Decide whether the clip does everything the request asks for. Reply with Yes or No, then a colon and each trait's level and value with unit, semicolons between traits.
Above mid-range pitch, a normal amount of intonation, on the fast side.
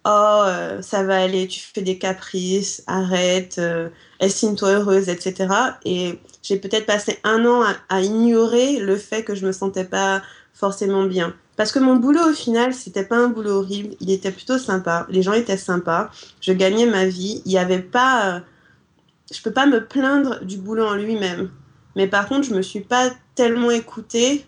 No: high, 200 Hz; average, 3.5 semitones; average, 190 wpm